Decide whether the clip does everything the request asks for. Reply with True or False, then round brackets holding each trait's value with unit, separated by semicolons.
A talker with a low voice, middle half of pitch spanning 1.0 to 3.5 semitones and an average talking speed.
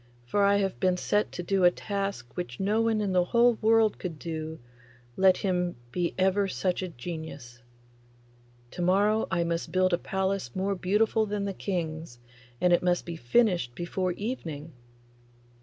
False (185 Hz; 2.9 semitones; 170 wpm)